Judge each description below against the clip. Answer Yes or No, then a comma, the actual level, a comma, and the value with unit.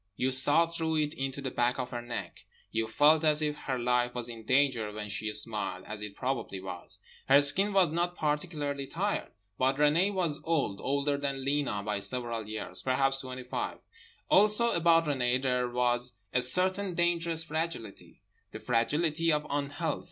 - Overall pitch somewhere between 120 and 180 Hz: Yes, low, 135 Hz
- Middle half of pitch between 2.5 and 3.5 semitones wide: No, average, 4.8 semitones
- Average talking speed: Yes, average, 175 wpm